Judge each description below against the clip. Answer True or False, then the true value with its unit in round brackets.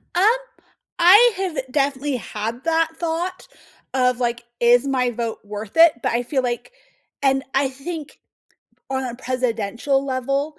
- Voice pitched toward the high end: True (265 Hz)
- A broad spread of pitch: False (3.9 semitones)